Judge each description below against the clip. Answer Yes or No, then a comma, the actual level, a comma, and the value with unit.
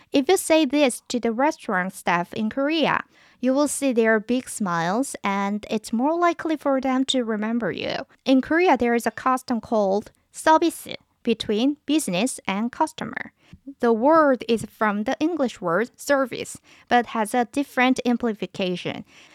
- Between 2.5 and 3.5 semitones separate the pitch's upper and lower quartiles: No, average, 4.3 semitones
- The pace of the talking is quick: No, average, 155 wpm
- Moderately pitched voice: No, very high, 250 Hz